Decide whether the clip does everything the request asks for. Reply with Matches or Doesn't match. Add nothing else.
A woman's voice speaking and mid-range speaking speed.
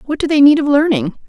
Doesn't match